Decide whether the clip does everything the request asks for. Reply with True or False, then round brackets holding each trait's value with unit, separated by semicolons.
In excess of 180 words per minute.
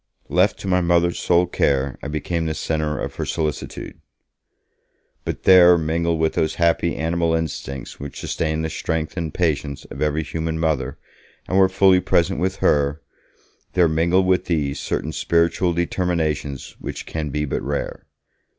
False (160 wpm)